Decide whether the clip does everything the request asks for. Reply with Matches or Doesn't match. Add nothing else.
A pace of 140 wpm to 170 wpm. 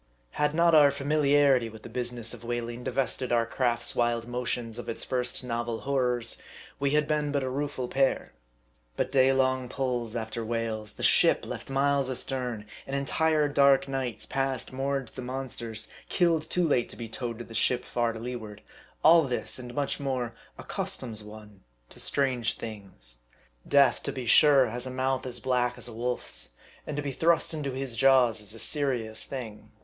Doesn't match